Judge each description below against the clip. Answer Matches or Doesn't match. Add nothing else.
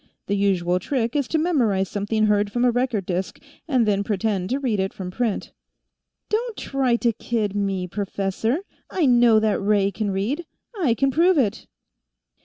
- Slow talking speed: Doesn't match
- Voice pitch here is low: Doesn't match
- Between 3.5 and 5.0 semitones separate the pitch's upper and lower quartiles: Matches